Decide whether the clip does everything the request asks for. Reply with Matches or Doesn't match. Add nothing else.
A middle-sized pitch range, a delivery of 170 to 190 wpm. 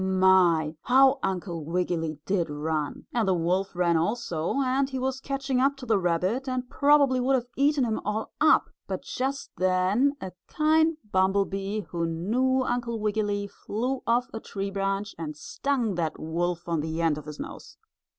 Doesn't match